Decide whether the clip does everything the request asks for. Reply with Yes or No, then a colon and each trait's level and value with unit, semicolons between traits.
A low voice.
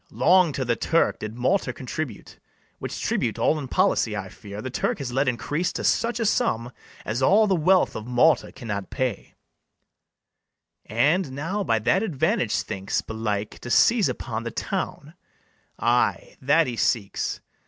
Yes: low, 130 Hz